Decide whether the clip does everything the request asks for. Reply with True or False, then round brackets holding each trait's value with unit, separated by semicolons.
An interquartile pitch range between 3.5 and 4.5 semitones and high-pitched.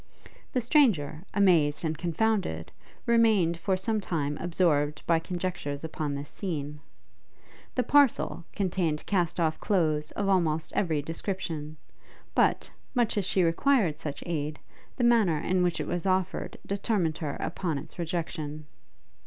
False (4.2 semitones; 170 Hz)